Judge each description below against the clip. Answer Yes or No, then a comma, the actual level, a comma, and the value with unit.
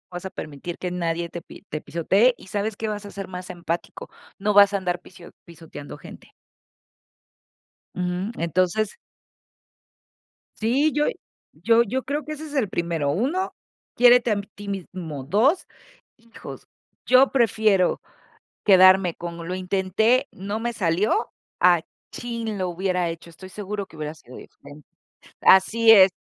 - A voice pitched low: No, high, 190 Hz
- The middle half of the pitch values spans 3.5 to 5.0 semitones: Yes, average, 4.5 semitones